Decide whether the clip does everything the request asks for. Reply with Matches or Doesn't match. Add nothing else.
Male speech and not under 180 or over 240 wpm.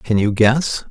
Matches